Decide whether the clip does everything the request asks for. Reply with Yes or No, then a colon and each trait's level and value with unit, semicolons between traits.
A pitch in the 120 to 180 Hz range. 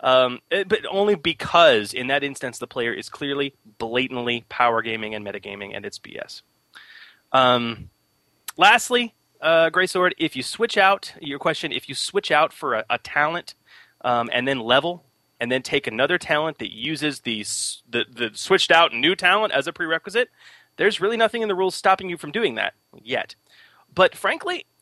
Yes: medium, 140 Hz